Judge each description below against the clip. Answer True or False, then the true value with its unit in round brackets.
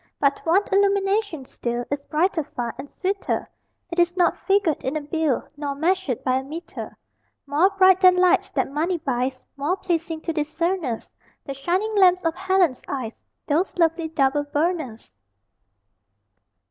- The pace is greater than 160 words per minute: False (150 wpm)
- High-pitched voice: True (325 Hz)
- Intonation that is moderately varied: True (4.7 semitones)